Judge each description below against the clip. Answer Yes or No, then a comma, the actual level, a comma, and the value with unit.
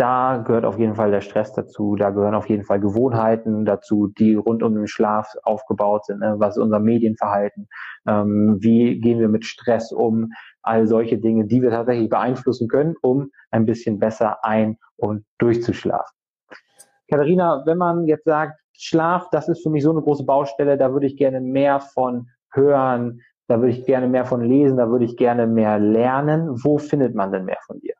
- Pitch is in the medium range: No, low, 120 Hz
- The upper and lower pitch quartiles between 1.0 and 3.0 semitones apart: No, average, 4.0 semitones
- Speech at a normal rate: No, fast, 195 wpm